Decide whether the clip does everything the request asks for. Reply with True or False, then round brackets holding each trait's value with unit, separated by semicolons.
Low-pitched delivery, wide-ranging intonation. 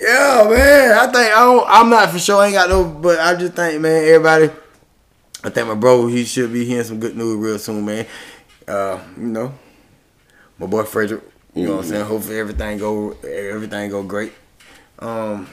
True (120 Hz; 8.5 semitones)